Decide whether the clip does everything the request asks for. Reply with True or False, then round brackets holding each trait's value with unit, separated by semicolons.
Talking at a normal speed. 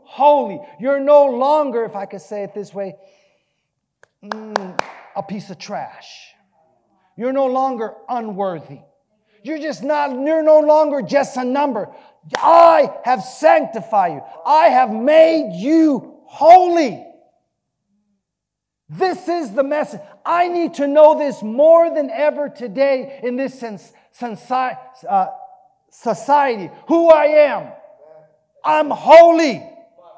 False (120 wpm)